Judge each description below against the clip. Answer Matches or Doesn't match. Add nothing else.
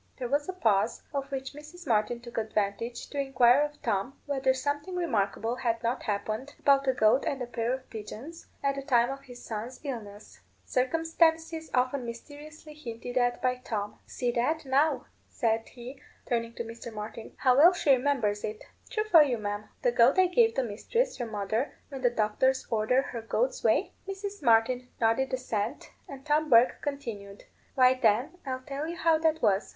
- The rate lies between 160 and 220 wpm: Matches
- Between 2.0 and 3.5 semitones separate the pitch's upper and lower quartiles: Doesn't match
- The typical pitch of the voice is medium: Doesn't match